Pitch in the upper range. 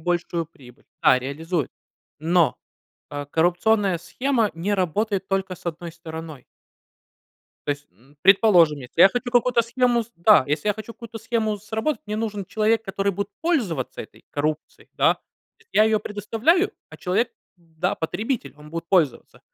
Yes: high, 195 Hz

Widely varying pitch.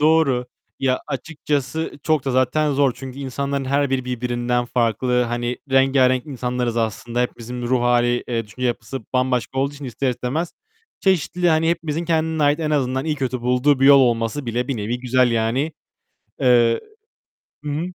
No: average, 2.8 semitones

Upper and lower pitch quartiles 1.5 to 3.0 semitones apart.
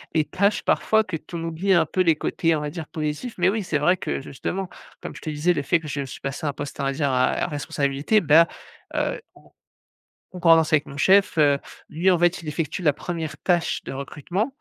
No: average, 3.4 semitones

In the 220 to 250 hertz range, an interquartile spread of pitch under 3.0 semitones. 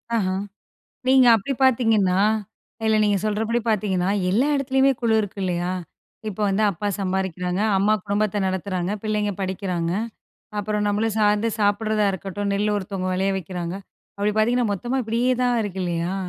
No: high, 205 Hz; narrow, 2.5 semitones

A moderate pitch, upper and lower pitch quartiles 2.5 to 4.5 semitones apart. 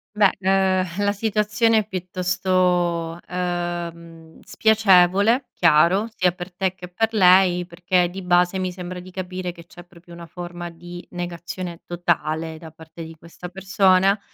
No: medium, 180 Hz; narrow, 1.7 semitones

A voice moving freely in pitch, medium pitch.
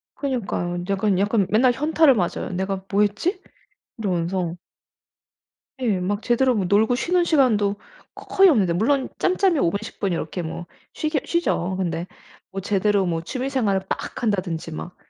No: wide, 5.8 semitones; high, 205 Hz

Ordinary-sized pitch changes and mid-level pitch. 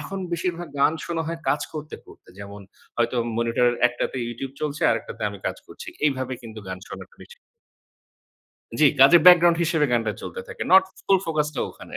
No: wide, 6.0 semitones; medium, 150 Hz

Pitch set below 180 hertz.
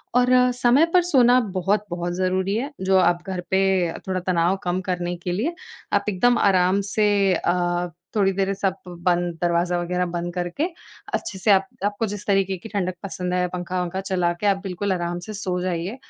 No: medium, 185 Hz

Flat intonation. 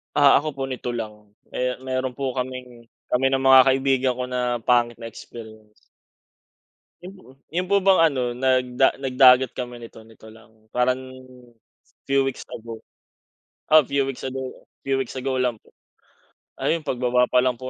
Yes: narrow, 1.8 semitones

